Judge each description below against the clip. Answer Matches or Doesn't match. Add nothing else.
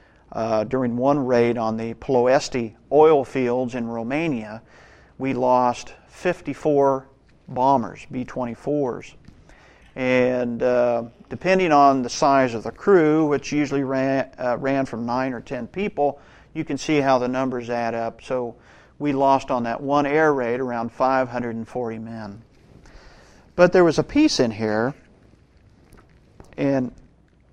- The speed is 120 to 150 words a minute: Matches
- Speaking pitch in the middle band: Doesn't match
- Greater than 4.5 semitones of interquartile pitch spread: Doesn't match